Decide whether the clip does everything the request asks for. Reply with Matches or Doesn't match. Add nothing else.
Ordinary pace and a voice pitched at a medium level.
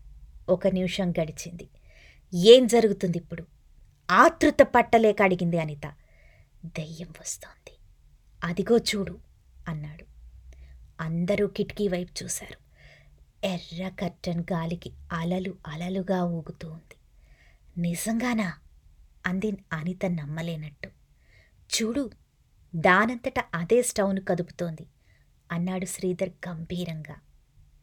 Matches